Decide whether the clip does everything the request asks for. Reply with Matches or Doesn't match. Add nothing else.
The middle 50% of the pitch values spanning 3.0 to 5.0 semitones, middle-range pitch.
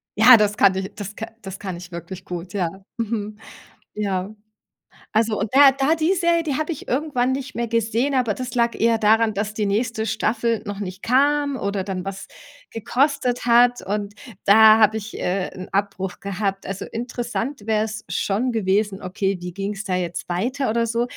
Doesn't match